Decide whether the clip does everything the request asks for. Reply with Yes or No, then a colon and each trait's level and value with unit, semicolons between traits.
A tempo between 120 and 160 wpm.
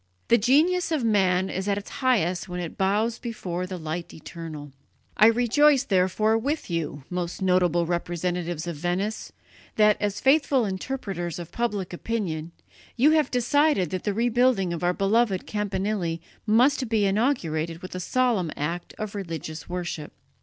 Yes: average, 155 wpm